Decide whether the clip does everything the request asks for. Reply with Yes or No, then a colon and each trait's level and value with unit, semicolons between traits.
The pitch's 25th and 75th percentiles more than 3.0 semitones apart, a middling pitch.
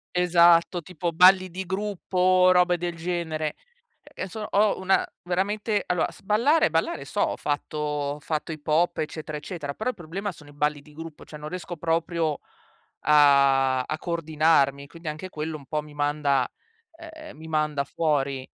Yes: average, 3.4 semitones; medium, 160 Hz